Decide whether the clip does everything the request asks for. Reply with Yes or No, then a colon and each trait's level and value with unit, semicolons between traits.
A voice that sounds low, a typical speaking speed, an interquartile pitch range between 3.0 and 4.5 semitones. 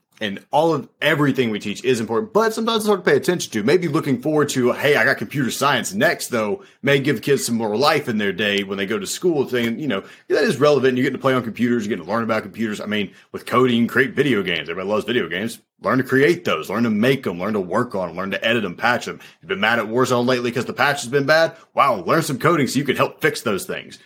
No: low, 130 Hz; fast, 280 wpm; average, 4.2 semitones